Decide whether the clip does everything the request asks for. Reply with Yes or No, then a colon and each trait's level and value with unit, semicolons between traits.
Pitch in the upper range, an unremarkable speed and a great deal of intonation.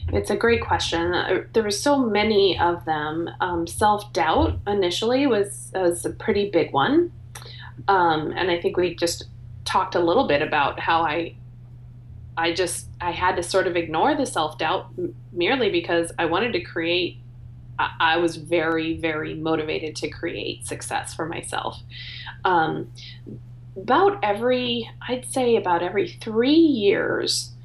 No: medium, 170 Hz; average, 150 wpm; wide, 8.8 semitones